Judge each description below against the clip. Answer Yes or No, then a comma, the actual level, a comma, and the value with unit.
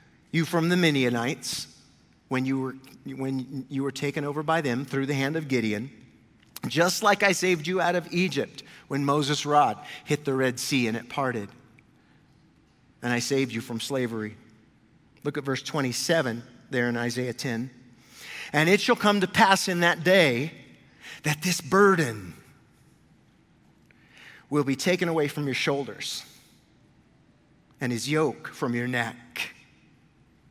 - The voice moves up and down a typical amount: Yes, average, 4.9 semitones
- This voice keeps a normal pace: Yes, average, 150 wpm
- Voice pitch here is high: No, medium, 140 Hz